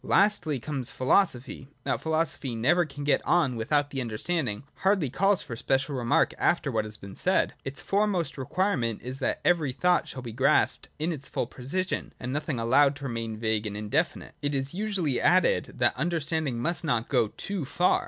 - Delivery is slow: No, average, 185 wpm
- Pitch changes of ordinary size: No, wide, 5.8 semitones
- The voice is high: No, medium, 140 Hz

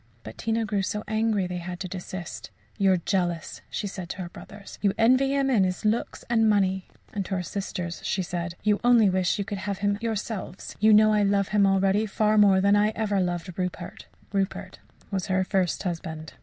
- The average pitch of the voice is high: Yes, high, 195 Hz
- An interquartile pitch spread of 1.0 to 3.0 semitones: Yes, narrow, 2.5 semitones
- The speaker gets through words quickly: Yes, fast, 210 wpm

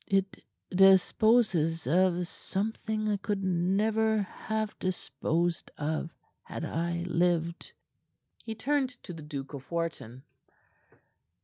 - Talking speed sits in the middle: No, slow, 105 wpm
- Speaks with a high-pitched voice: No, medium, 180 Hz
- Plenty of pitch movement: No, average, 4.4 semitones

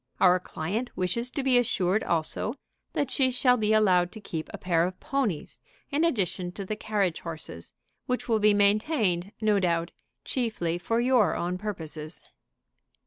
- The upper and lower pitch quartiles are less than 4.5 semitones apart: No, average, 5.0 semitones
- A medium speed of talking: Yes, average, 160 wpm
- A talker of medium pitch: No, high, 205 Hz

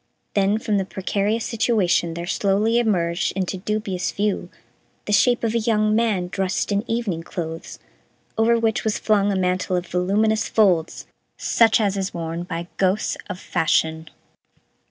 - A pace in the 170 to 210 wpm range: No, average, 155 wpm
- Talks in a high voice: Yes, high, 200 Hz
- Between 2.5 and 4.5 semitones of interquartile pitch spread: Yes, average, 3.2 semitones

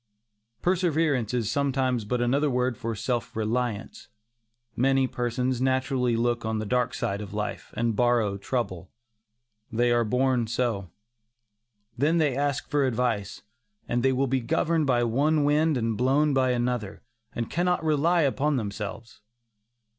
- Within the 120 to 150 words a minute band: Yes, average, 145 wpm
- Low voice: Yes, low, 125 Hz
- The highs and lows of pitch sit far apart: No, average, 3.3 semitones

